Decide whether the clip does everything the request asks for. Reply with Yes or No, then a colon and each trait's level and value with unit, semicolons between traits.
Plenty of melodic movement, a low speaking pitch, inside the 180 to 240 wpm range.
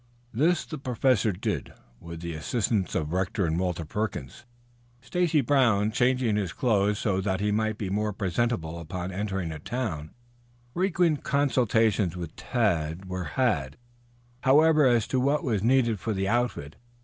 No: wide, 5.8 semitones; low, 105 Hz; average, 150 wpm